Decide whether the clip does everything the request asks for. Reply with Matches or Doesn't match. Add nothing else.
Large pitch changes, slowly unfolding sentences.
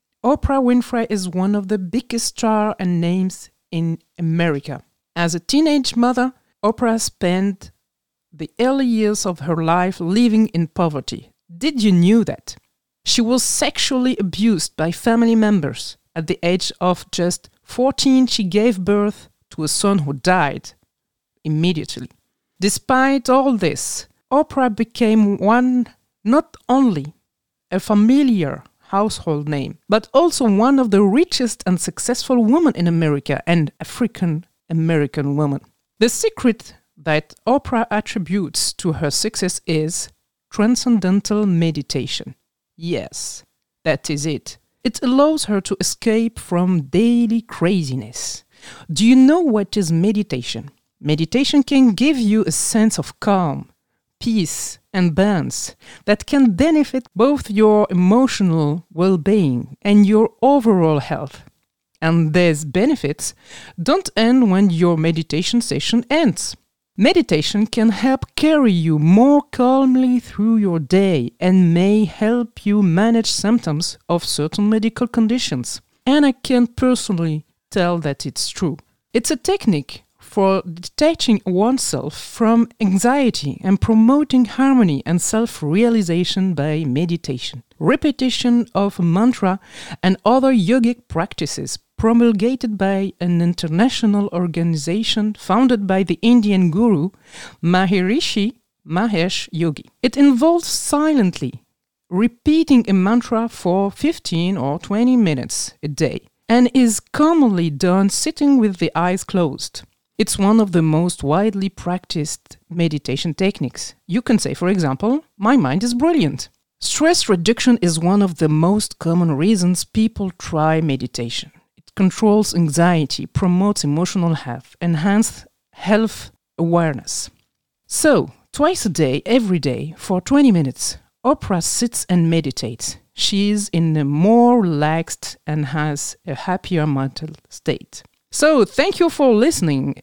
Matches